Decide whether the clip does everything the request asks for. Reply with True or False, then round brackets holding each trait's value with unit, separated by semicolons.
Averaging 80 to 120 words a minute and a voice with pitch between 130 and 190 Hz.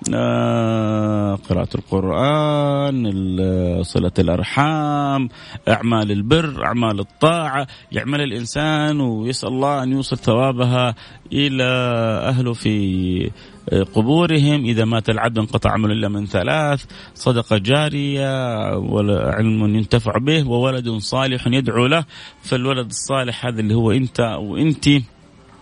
False (100 wpm; 120 Hz)